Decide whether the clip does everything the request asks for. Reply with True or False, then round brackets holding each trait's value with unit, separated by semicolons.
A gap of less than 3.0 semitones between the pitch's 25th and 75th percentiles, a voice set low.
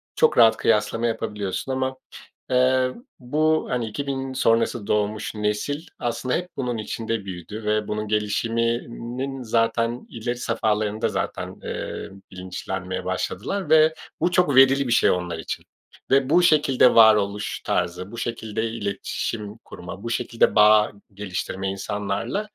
False (3.8 semitones; 115 Hz)